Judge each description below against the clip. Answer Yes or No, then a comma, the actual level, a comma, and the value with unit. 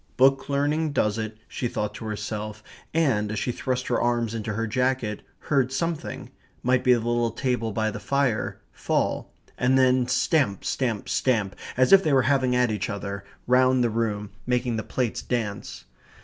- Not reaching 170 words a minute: No, average, 175 wpm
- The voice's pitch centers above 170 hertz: No, low, 120 Hz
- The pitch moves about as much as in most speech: Yes, average, 3.2 semitones